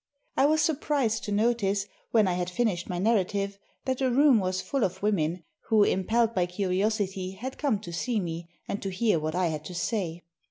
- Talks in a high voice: Yes, high, 200 Hz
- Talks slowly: No, average, 200 wpm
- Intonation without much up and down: No, average, 4.3 semitones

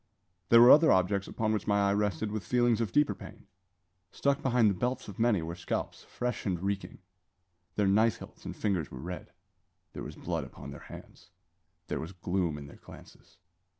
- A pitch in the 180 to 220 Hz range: No, low, 100 Hz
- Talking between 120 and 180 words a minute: No, average, 190 wpm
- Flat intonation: No, average, 4.2 semitones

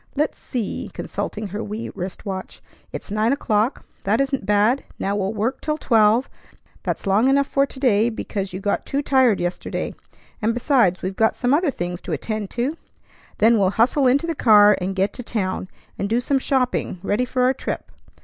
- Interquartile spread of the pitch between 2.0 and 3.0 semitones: No, average, 4.5 semitones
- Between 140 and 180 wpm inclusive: No, average, 190 wpm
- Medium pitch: No, high, 225 Hz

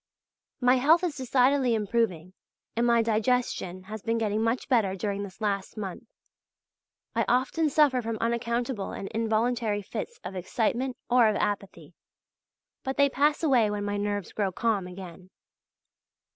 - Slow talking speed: No, average, 145 wpm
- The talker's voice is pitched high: Yes, high, 225 Hz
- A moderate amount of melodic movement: Yes, average, 3.6 semitones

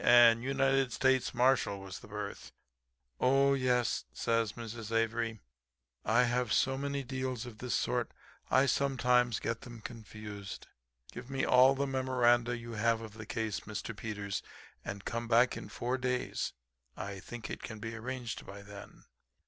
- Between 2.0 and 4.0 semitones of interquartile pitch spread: Yes, narrow, 2.6 semitones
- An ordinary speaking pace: Yes, average, 155 wpm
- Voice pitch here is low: Yes, low, 120 Hz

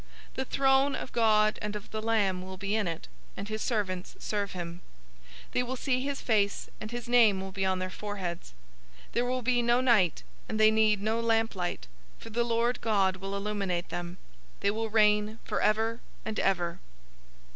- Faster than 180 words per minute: Yes, average, 190 wpm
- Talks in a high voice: Yes, high, 215 Hz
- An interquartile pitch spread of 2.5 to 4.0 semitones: Yes, average, 3.2 semitones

